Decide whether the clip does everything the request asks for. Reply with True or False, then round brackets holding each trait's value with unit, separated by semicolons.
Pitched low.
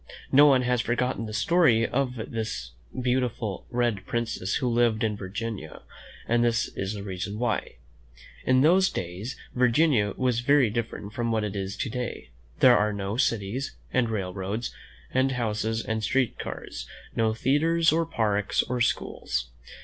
True (115 Hz)